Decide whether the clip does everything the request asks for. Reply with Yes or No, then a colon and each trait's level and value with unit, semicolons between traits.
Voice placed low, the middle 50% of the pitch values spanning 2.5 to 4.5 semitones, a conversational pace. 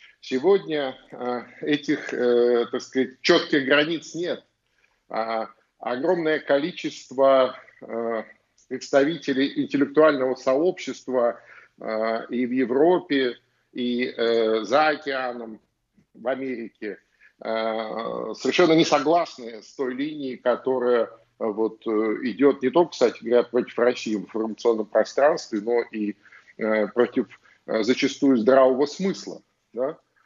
No: low, 130 Hz; average, 3.8 semitones; slow, 85 wpm